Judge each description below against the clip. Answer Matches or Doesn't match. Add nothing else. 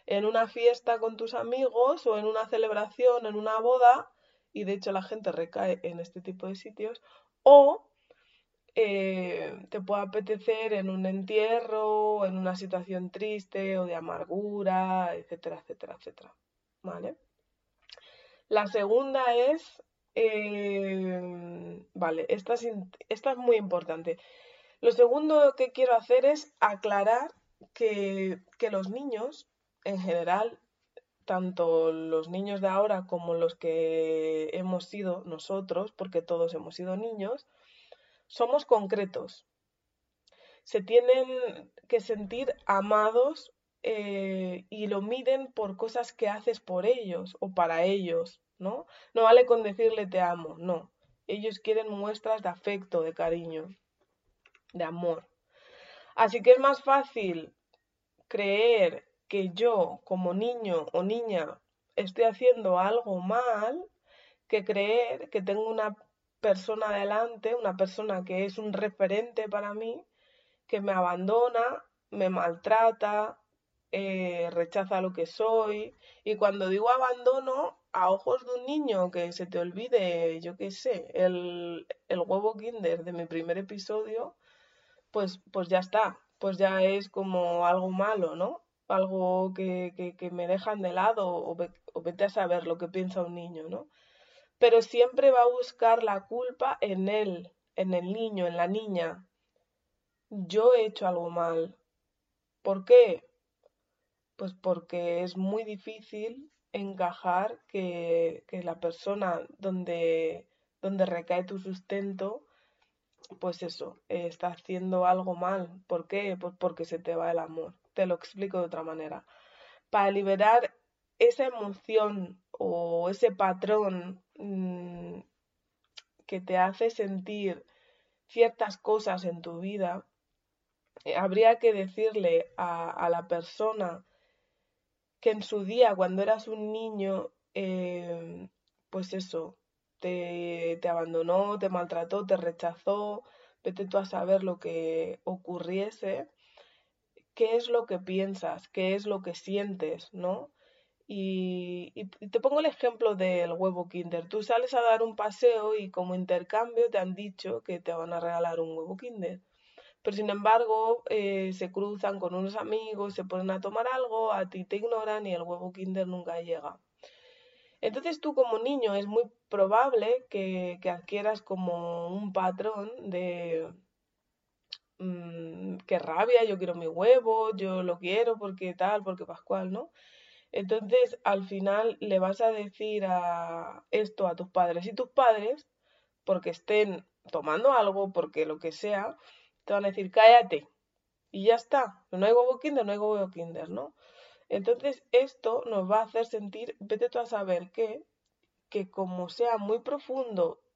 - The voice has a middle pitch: Doesn't match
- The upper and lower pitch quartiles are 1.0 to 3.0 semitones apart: Doesn't match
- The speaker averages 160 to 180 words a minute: Doesn't match